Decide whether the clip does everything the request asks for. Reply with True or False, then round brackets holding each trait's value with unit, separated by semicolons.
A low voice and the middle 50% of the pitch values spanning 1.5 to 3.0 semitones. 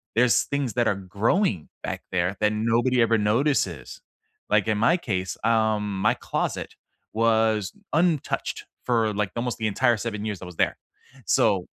True (110 Hz; 2.4 semitones)